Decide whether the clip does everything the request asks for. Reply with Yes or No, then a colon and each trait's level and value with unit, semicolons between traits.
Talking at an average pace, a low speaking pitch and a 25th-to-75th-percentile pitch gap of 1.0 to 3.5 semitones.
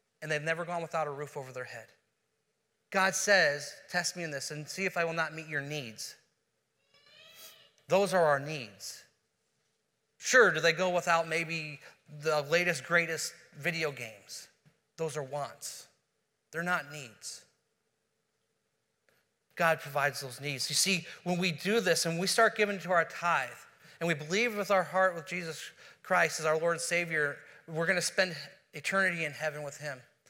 No: average, 170 wpm; medium, 165 Hz; average, 2.9 semitones